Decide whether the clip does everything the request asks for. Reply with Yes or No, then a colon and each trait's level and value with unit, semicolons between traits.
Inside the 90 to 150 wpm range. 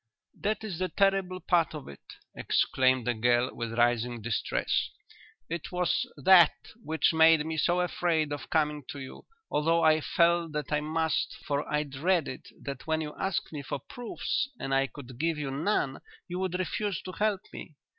No: average, 175 wpm